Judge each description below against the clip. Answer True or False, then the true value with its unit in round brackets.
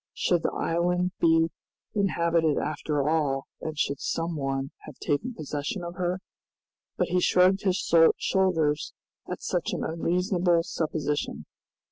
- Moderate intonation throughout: True (3.2 semitones)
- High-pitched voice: False (165 Hz)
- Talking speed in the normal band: False (130 wpm)